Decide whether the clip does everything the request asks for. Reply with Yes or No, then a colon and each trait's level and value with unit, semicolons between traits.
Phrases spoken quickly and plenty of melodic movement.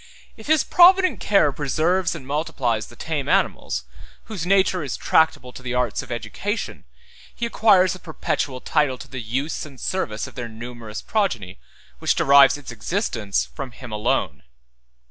No: average, 160 wpm; wide, 7.4 semitones